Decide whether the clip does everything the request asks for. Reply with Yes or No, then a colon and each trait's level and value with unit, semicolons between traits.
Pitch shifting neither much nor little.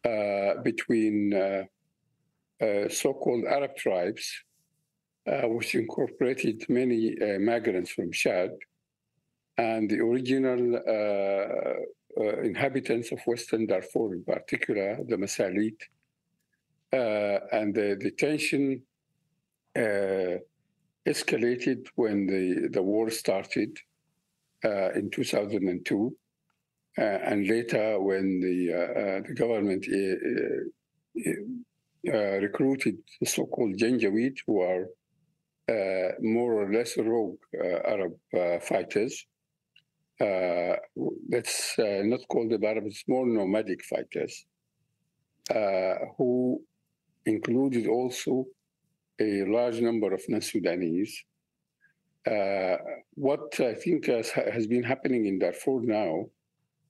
No: wide, 6.8 semitones